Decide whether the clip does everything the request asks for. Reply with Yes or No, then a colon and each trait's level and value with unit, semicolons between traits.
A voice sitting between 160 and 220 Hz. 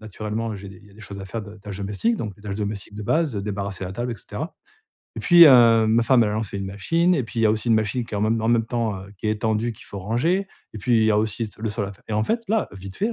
No: low, 110 Hz